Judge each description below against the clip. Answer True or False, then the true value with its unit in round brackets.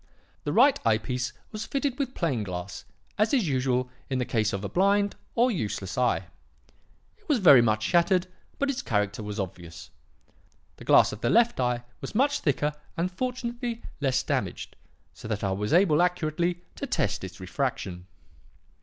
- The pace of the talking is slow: False (170 wpm)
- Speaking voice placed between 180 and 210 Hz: False (140 Hz)